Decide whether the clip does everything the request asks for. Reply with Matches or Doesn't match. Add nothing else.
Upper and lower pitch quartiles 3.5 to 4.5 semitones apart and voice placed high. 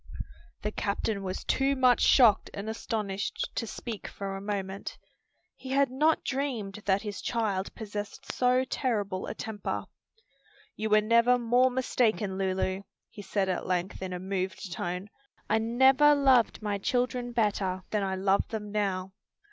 Matches